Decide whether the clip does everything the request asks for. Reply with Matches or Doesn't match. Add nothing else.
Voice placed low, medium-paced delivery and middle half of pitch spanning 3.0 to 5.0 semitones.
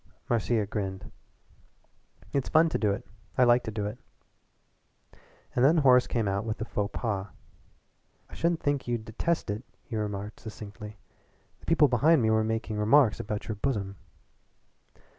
Matches